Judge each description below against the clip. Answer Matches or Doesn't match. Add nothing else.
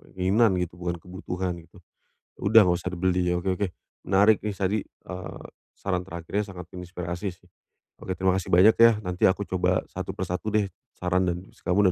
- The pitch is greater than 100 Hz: Doesn't match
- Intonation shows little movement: Matches